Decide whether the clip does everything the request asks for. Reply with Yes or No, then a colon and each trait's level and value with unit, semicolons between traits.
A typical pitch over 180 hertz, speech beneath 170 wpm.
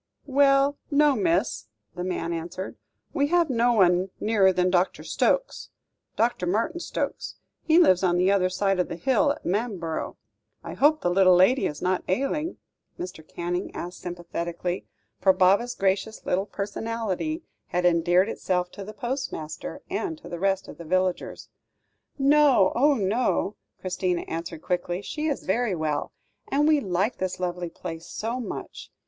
Yes: high, 190 Hz; average, 155 wpm